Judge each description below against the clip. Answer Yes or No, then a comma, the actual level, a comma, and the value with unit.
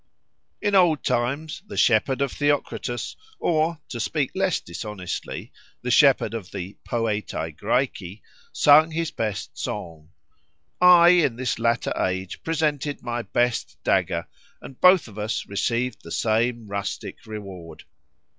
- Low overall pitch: Yes, low, 120 Hz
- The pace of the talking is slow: Yes, slow, 130 wpm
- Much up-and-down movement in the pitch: Yes, wide, 6.4 semitones